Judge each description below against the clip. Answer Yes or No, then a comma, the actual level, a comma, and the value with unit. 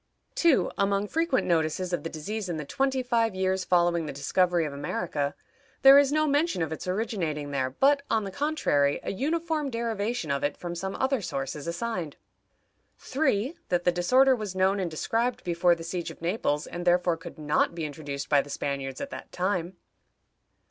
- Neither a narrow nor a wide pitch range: No, wide, 6.7 semitones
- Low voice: No, medium, 180 Hz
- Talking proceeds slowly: No, average, 190 wpm